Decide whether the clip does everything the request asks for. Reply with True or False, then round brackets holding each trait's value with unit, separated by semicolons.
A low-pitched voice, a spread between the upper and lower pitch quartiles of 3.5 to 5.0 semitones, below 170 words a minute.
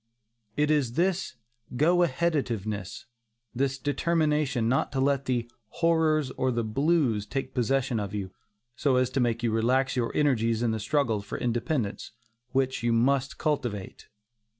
True (130 Hz; 4.1 semitones; 150 wpm)